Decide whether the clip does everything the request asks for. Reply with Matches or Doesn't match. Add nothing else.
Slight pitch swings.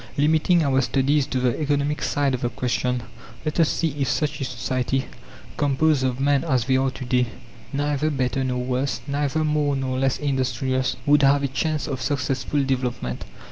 Matches